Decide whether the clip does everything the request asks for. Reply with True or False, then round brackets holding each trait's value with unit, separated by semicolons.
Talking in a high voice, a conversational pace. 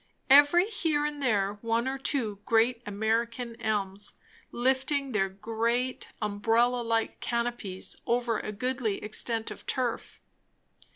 False (235 Hz; 120 wpm)